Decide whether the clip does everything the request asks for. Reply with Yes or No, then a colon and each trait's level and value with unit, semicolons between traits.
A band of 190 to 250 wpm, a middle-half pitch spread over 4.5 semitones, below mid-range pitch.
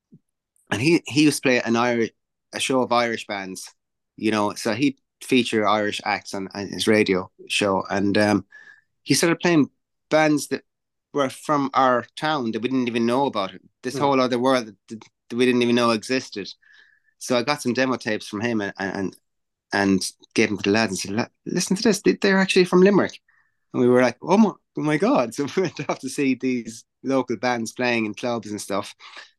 Yes: fast, 205 wpm; average, 4.9 semitones; low, 125 Hz